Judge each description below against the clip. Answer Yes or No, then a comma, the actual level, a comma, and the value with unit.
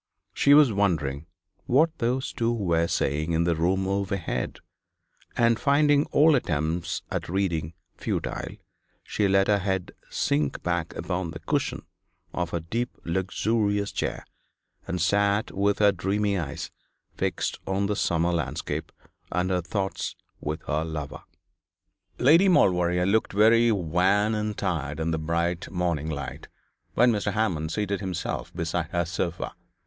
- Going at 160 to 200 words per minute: No, average, 140 wpm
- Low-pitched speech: Yes, very low, 95 Hz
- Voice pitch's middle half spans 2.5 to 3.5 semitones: No, average, 3.9 semitones